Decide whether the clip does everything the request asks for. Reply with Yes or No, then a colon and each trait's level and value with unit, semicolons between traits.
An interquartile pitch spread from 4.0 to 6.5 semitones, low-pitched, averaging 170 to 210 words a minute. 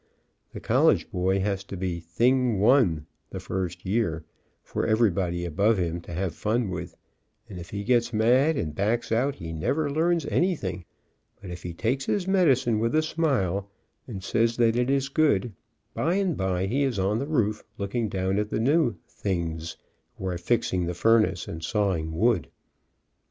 Yes: wide, 5.4 semitones; low, 105 Hz; average, 185 wpm